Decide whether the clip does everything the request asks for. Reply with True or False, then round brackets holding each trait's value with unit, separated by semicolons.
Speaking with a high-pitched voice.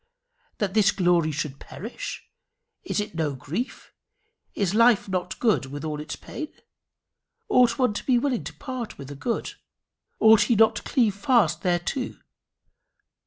True (205 Hz)